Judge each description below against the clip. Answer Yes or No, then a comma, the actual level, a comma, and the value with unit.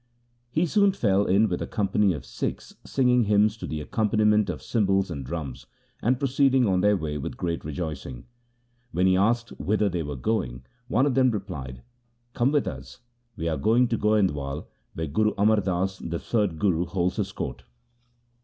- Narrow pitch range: No, wide, 5.4 semitones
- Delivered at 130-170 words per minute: No, average, 185 wpm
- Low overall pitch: Yes, low, 100 Hz